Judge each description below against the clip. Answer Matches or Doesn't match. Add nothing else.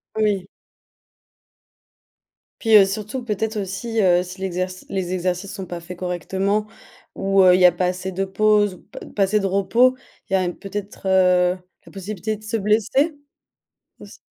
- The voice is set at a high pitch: Matches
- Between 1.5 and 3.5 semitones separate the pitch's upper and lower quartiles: Matches